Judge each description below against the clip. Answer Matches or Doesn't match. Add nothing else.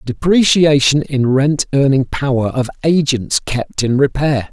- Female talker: Doesn't match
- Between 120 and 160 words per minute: Matches